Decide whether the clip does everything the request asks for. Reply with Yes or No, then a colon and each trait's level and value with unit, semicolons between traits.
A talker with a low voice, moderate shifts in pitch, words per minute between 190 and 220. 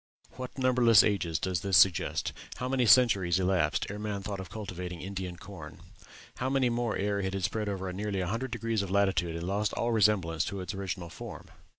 Yes: low, 100 Hz; average, 3.2 semitones; average, 200 wpm